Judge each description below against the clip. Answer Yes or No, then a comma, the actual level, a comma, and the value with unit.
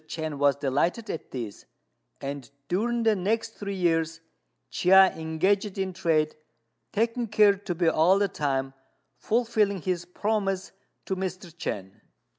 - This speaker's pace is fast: No, slow, 135 wpm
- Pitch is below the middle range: No, medium, 185 Hz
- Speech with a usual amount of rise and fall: Yes, average, 4.4 semitones